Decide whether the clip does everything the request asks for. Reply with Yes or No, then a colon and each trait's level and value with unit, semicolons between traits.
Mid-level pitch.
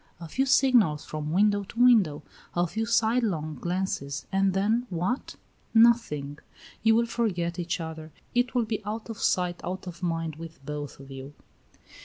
Yes: medium, 180 Hz